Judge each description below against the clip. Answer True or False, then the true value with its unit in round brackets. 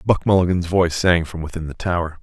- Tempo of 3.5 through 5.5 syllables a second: False (6.3 syllables/s)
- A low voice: True (85 Hz)